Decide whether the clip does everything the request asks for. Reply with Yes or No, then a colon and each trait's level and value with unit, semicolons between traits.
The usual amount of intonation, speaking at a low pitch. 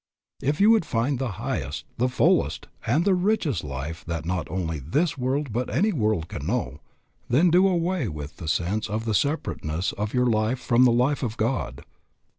No: wide, 8.3 semitones; low, 120 Hz